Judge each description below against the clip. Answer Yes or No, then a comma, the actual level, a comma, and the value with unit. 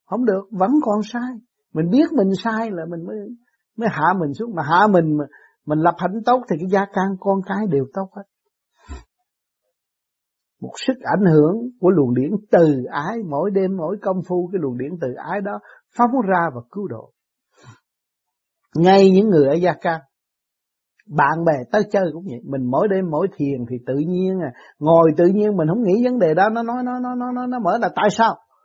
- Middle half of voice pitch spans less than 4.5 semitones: No, average, 5.2 semitones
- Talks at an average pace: Yes, average, 205 wpm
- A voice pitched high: Yes, high, 195 Hz